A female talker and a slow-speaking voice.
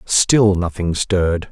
No: male; slow, 120 wpm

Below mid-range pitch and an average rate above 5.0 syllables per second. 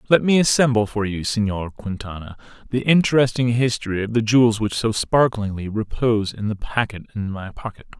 Yes: low, 115 Hz; 5.6 syllables/s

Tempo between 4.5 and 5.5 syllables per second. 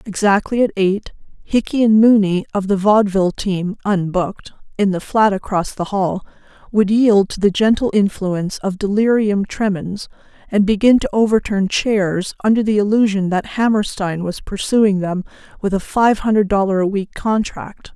Yes: 4.9 syllables/s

